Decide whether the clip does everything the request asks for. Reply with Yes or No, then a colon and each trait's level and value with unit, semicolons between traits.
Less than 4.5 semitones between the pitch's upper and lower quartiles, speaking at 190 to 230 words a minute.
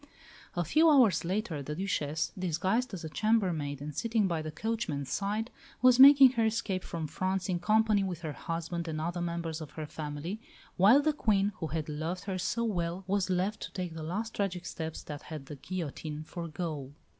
No: average, 4.8 semitones; average, 195 wpm